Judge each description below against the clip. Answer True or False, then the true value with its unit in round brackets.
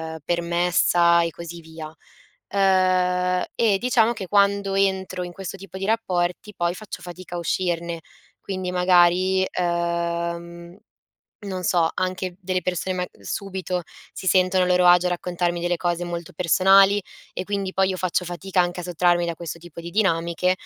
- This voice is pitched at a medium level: True (180 Hz)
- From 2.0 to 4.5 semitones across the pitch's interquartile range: False (1.6 semitones)